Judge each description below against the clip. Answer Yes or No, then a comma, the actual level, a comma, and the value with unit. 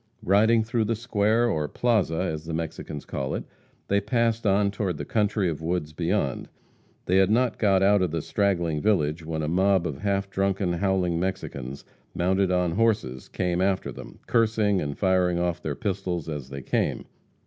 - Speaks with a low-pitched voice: Yes, very low, 95 Hz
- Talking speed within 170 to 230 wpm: Yes, average, 180 wpm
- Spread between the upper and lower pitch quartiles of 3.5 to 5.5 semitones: Yes, average, 3.9 semitones